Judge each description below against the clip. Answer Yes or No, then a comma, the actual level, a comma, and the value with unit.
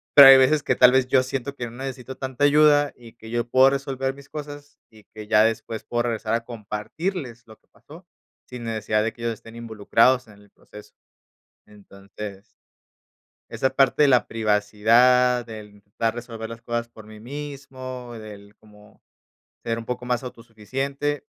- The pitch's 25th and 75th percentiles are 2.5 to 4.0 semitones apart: Yes, average, 3.4 semitones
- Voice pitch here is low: Yes, low, 120 Hz